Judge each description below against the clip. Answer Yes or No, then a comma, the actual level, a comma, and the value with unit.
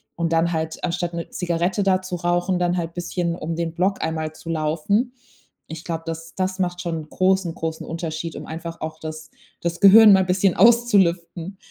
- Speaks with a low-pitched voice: No, medium, 170 Hz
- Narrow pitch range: Yes, narrow, 2.2 semitones